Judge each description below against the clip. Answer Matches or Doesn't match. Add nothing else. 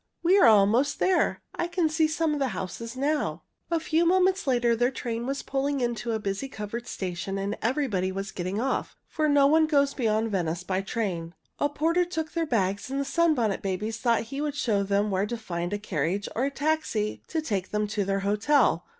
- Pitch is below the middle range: Doesn't match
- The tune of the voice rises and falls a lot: Matches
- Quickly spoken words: Matches